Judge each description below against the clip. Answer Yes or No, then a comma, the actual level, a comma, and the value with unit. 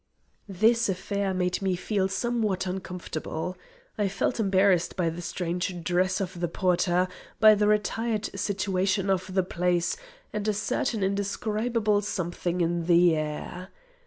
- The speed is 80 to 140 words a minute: Yes, slow, 135 wpm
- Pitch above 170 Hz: Yes, high, 190 Hz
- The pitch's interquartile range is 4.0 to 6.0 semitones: No, narrow, 2.5 semitones